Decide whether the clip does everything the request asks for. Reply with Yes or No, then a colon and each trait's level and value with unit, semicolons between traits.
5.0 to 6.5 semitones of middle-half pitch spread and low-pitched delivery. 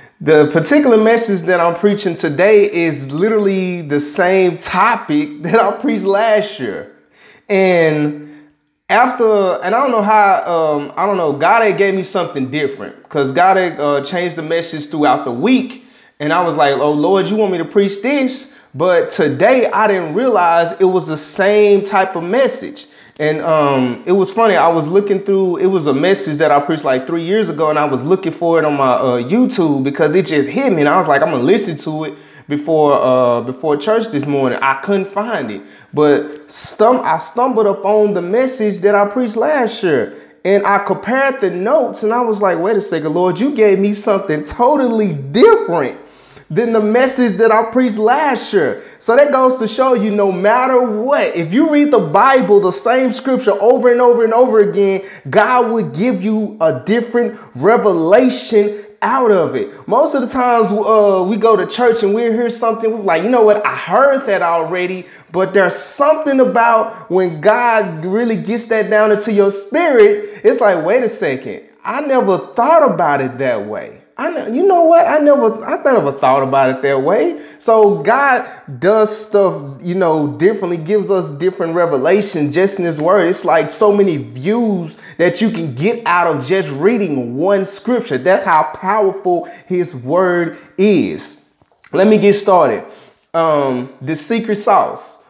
No: wide, 5.5 semitones; high, 195 Hz